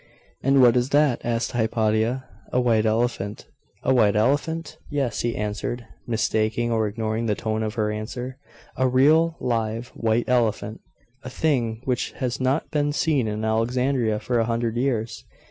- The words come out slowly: No, average, 160 wpm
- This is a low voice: Yes, low, 120 Hz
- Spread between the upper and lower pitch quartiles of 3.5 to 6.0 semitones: No, average, 2.8 semitones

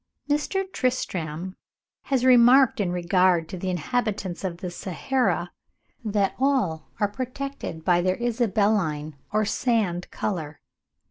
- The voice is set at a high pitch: Yes, high, 200 Hz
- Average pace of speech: No, slow, 120 wpm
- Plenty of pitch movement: Yes, wide, 5.9 semitones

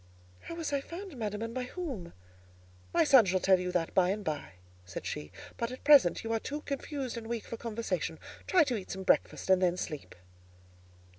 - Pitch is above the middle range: Yes, high, 225 Hz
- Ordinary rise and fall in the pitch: No, wide, 7.0 semitones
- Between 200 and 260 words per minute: Yes, fast, 205 wpm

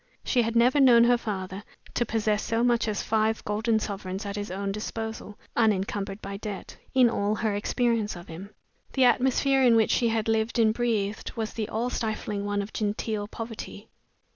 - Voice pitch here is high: Yes, high, 220 Hz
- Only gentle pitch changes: Yes, narrow, 2.3 semitones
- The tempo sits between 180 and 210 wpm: Yes, average, 185 wpm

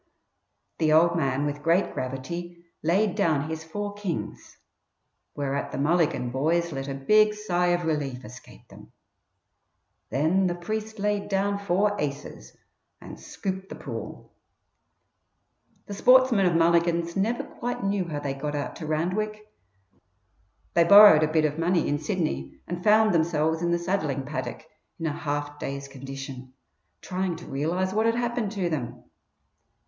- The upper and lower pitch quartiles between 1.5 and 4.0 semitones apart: No, average, 5.1 semitones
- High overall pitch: No, medium, 170 Hz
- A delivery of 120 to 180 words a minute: Yes, average, 150 wpm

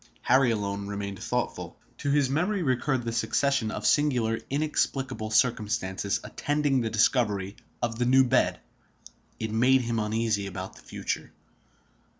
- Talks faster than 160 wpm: No, average, 140 wpm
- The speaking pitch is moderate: No, low, 115 Hz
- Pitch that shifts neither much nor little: Yes, average, 3.9 semitones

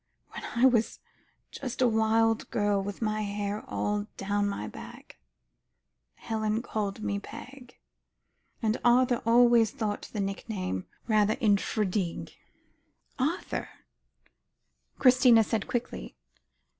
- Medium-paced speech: No, slow, 110 wpm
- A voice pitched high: Yes, high, 215 Hz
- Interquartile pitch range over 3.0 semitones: No, narrow, 2.6 semitones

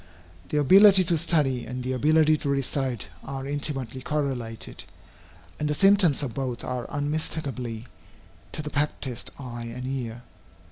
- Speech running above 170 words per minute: No, average, 140 wpm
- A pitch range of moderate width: Yes, average, 3.1 semitones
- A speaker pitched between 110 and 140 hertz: Yes, low, 135 Hz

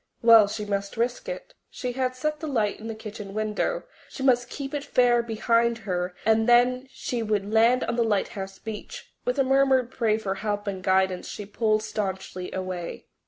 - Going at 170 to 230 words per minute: Yes, average, 190 wpm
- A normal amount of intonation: Yes, average, 3.6 semitones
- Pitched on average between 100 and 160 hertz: No, high, 225 Hz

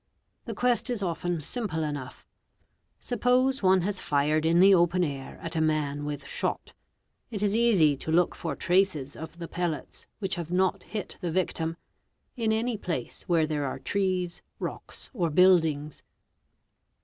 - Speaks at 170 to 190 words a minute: No, average, 160 wpm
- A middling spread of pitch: Yes, average, 4.3 semitones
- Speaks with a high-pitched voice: No, medium, 175 Hz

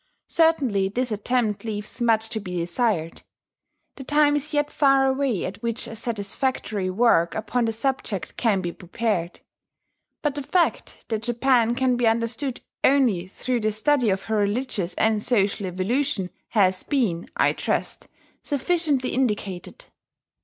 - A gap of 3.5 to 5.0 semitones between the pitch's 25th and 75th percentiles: Yes, average, 4.7 semitones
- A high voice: Yes, high, 230 Hz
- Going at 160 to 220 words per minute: No, average, 145 wpm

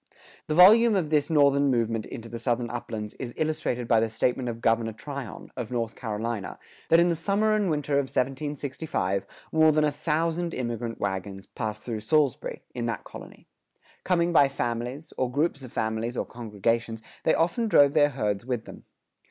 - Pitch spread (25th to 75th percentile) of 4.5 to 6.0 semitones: Yes, average, 5.0 semitones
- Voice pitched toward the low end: Yes, low, 125 Hz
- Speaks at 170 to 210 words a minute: Yes, average, 175 wpm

